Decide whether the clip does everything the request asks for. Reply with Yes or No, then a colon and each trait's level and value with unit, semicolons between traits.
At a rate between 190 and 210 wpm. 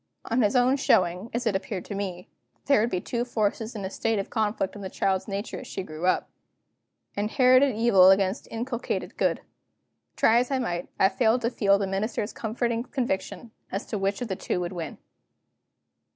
Yes: average, 195 wpm